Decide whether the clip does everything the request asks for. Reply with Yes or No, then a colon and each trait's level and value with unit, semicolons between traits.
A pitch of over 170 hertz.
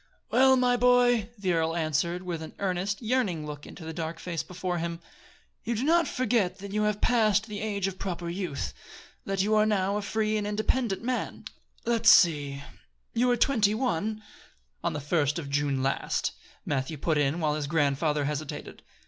Yes: medium, 185 Hz